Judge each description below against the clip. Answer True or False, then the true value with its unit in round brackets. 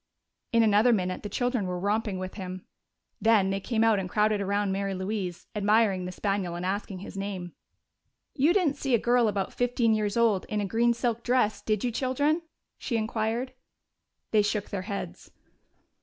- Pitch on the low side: False (210 Hz)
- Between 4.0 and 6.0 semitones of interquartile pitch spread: False (3.2 semitones)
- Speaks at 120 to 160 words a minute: False (180 wpm)